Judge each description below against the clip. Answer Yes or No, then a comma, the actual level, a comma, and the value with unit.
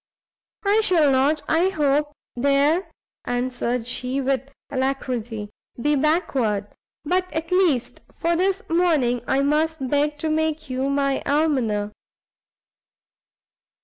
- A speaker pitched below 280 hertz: No, very high, 285 Hz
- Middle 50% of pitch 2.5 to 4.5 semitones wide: Yes, average, 3.7 semitones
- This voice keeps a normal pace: No, slow, 115 wpm